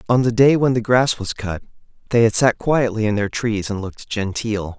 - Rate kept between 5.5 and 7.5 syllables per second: No, 5.1 syllables/s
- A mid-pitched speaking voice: No, low, 110 Hz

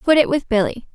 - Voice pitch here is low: No, very high, 265 Hz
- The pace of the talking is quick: Yes, fast, 255 wpm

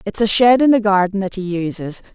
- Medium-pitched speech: No, high, 200 Hz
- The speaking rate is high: Yes, fast, 250 wpm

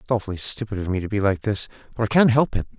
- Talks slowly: No, fast, 300 wpm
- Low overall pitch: Yes, low, 105 Hz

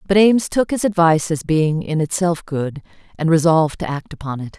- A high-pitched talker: No, medium, 165 Hz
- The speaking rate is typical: No, fast, 210 wpm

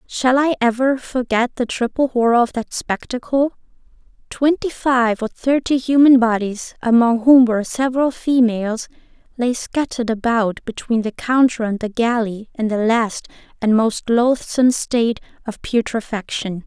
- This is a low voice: No, high, 240 Hz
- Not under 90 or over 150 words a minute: Yes, average, 140 wpm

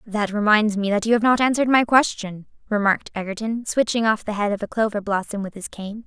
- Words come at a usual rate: No, fast, 230 wpm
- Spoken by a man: No, female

